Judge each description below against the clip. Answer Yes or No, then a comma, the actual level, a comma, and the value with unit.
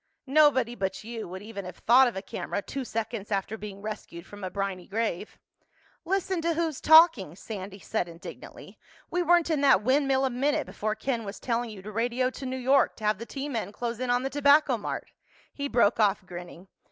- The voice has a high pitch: Yes, high, 230 Hz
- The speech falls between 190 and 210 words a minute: Yes, fast, 205 wpm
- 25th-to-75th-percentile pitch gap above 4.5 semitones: Yes, average, 5.2 semitones